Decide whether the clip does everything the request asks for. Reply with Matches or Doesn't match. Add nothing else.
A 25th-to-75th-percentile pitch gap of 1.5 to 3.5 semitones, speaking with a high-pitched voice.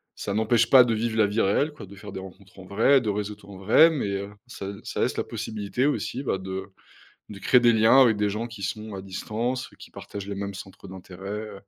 Doesn't match